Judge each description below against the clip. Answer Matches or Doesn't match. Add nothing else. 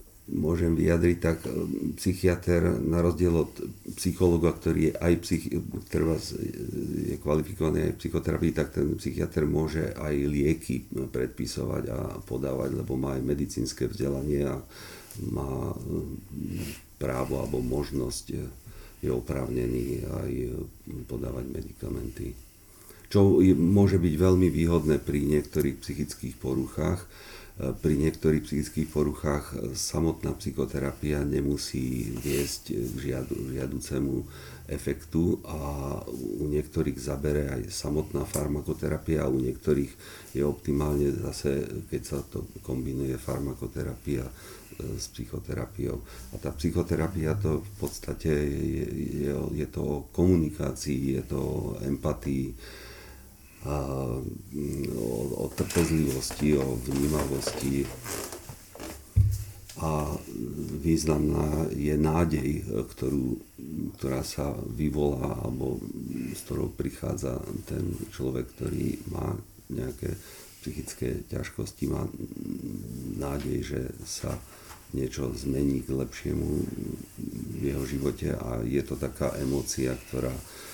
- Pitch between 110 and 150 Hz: Doesn't match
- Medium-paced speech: Doesn't match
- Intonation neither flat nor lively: Matches